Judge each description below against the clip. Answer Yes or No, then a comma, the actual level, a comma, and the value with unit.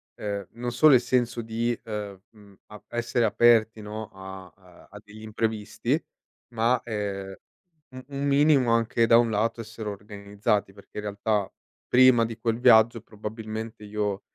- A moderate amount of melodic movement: No, narrow, 2.3 semitones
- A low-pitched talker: Yes, low, 110 Hz